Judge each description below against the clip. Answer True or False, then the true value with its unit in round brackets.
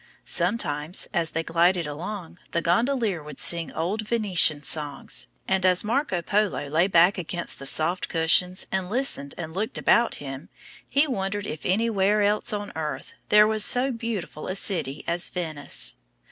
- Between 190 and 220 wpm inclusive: False (160 wpm)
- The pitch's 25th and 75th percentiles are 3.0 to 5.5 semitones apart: True (4.6 semitones)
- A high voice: False (180 Hz)